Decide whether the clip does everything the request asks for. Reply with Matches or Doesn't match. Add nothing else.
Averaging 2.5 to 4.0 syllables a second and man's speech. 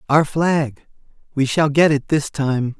Matches